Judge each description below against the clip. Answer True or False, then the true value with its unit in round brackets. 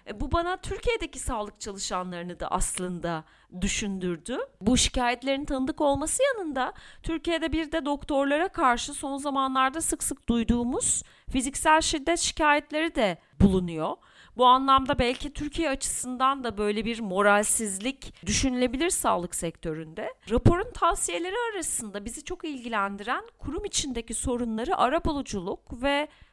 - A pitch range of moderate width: False (6.1 semitones)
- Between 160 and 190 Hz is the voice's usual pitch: False (265 Hz)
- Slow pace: True (120 wpm)